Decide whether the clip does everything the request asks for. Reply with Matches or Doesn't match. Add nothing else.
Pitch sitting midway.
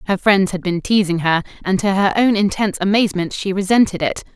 Doesn't match